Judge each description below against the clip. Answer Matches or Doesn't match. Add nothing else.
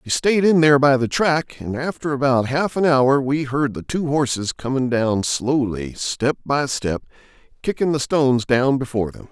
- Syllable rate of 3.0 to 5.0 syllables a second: Matches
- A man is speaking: Matches